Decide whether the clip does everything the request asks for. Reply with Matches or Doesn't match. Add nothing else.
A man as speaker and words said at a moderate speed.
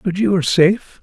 Matches